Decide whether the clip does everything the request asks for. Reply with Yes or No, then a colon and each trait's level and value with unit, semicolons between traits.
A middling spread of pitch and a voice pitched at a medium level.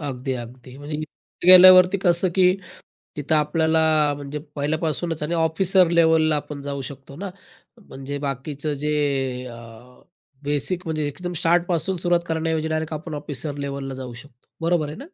Yes: average, 3.1 semitones; medium, 155 Hz